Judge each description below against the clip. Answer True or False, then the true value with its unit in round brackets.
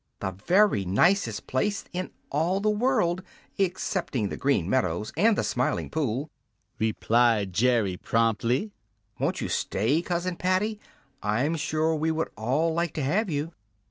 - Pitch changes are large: True (8.0 semitones)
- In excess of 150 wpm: False (140 wpm)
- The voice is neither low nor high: True (150 Hz)